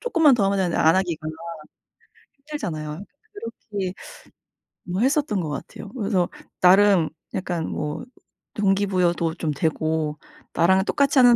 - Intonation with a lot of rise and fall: No, average, 4.2 semitones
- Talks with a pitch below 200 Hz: Yes, high, 190 Hz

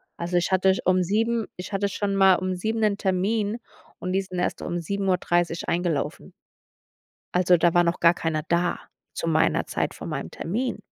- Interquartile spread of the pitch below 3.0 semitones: Yes, narrow, 2.5 semitones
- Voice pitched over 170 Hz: Yes, medium, 185 Hz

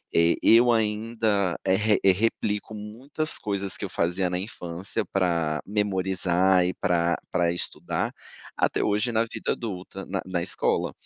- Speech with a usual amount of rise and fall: Yes, average, 3.2 semitones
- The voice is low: Yes, very low, 95 Hz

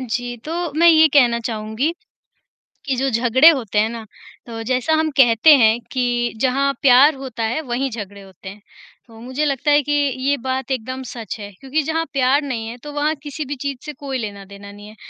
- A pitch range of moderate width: Yes, average, 4.0 semitones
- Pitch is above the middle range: Yes, very high, 255 Hz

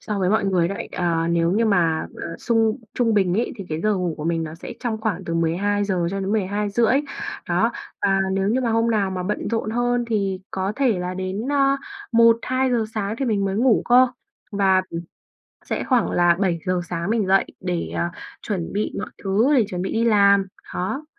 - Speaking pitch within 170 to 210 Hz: Yes, high, 200 Hz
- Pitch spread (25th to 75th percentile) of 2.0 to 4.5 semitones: Yes, average, 3.8 semitones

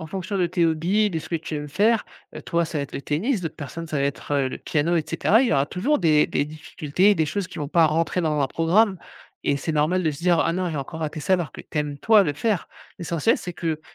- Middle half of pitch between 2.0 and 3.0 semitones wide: No, average, 3.5 semitones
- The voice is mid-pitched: Yes, medium, 165 Hz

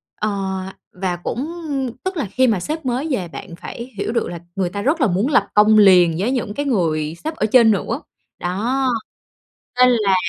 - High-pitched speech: Yes, high, 215 Hz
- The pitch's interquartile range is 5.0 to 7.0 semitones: Yes, wide, 5.6 semitones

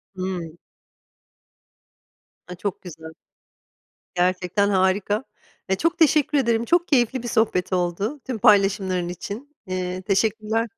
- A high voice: Yes, high, 200 Hz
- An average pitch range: Yes, average, 4.2 semitones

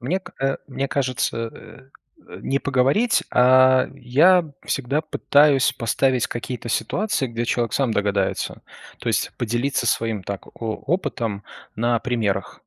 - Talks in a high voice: No, low, 125 Hz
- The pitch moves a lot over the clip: No, average, 3.2 semitones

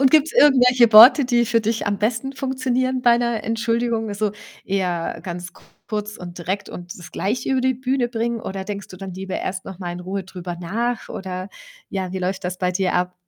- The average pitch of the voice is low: No, high, 210 Hz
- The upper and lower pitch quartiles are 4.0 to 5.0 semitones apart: Yes, average, 4.6 semitones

